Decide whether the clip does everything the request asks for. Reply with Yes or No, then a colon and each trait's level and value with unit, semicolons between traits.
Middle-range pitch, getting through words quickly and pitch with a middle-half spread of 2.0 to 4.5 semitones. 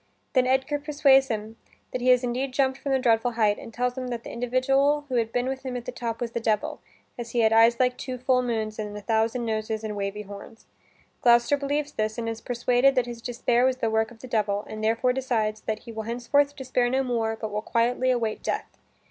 No: high, 240 Hz; fast, 235 wpm; narrow, 2.6 semitones